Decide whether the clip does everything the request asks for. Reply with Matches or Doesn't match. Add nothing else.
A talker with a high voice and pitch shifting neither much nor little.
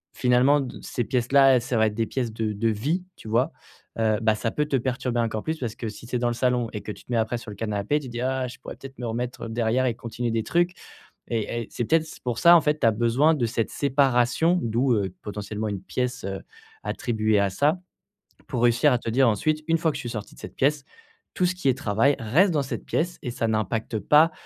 Doesn't match